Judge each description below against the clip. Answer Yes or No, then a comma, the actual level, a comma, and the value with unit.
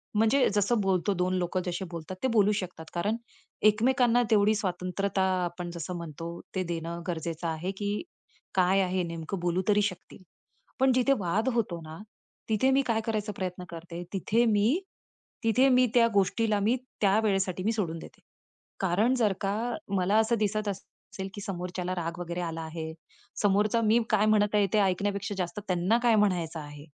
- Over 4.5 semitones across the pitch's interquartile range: No, average, 3.6 semitones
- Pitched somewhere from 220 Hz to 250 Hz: No, high, 195 Hz